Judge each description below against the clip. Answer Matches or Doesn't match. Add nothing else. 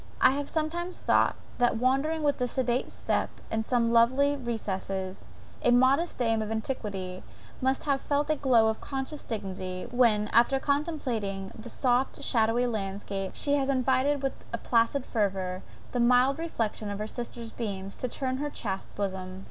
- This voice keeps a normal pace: Matches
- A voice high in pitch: Matches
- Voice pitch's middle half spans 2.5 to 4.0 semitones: Doesn't match